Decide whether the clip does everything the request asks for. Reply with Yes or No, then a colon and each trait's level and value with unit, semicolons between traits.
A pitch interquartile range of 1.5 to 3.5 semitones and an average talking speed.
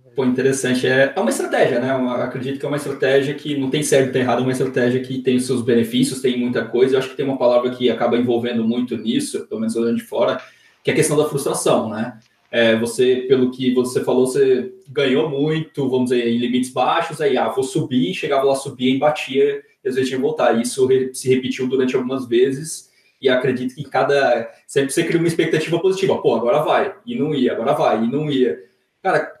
No: narrow, 2.6 semitones; fast, 225 wpm